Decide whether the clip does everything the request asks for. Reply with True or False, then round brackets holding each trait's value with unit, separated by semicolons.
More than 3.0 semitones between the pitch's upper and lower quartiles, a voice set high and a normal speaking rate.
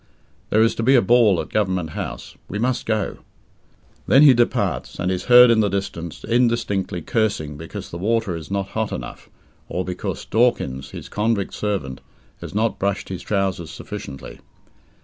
False (4.2 semitones; 100 Hz; 170 wpm)